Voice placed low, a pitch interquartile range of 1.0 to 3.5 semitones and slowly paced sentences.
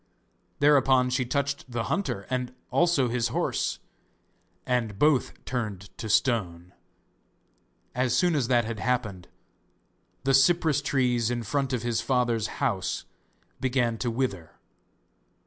Yes: low, 125 Hz; average, 2.7 semitones; slow, 125 wpm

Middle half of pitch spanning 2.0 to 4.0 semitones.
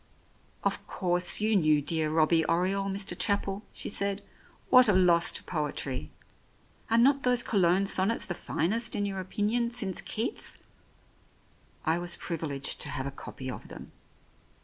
No: average, 4.4 semitones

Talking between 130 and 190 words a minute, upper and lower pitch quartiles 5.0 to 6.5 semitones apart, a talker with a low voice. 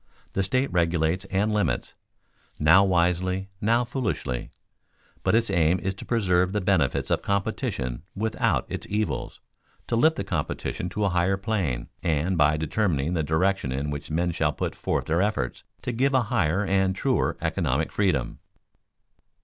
No: average, 155 wpm; average, 4.3 semitones; very low, 95 Hz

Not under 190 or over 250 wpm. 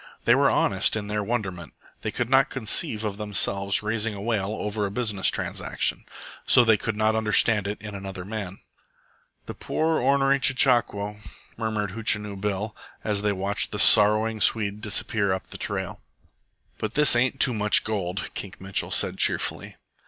No: average, 165 wpm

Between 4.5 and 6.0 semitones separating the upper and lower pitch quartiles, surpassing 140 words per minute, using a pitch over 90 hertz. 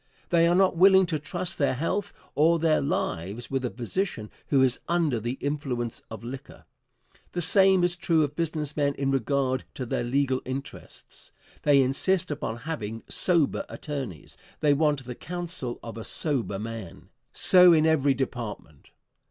Yes: average, 5.2 semitones; average, 160 wpm; medium, 140 Hz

